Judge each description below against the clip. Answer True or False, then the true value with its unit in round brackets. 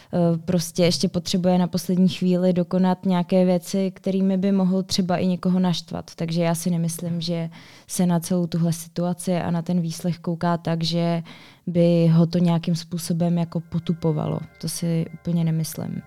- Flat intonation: True (1.4 semitones)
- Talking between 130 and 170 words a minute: True (165 wpm)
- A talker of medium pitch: True (175 Hz)